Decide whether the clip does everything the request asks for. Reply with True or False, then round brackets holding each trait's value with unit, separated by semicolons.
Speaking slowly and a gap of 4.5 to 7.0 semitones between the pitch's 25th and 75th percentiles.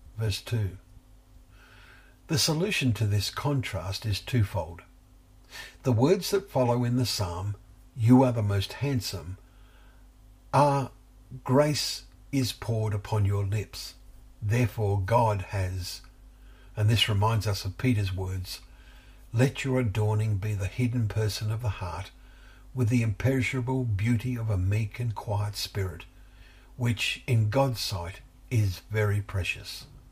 True (130 wpm; 4.8 semitones)